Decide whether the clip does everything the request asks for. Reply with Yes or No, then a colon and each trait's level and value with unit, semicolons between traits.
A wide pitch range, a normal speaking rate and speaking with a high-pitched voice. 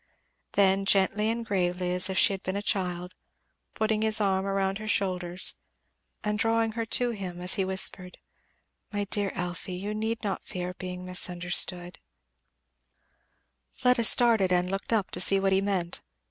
No: average, 2.7 semitones; average, 160 wpm; high, 195 Hz